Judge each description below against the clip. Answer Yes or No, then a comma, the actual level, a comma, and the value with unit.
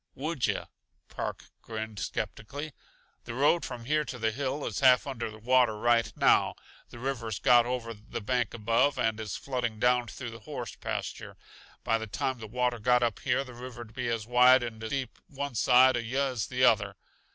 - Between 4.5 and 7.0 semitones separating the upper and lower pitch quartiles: No, narrow, 2.4 semitones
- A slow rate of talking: No, average, 190 wpm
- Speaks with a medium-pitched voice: No, low, 120 Hz